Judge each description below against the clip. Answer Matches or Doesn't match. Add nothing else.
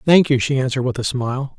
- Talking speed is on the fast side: Matches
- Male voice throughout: Matches